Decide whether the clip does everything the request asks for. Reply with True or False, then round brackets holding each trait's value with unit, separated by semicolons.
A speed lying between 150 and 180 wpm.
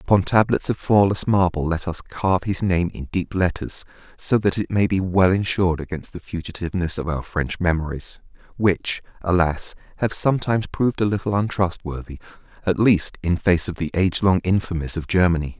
True (175 wpm)